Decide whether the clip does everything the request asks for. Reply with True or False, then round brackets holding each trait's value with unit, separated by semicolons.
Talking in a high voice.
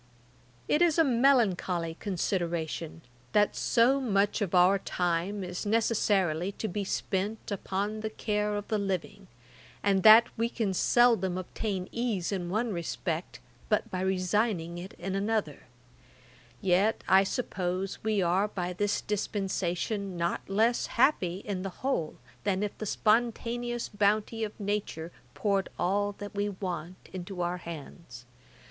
True (200 Hz)